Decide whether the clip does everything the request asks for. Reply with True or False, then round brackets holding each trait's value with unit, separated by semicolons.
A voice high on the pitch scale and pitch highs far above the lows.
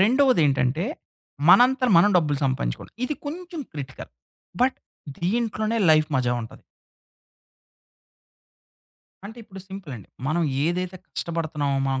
False (175 Hz; 8.2 semitones)